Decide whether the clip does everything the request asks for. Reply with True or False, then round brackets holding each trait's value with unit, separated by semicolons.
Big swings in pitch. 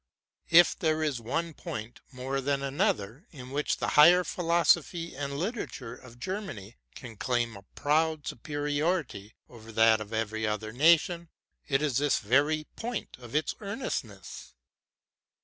True (6.2 semitones)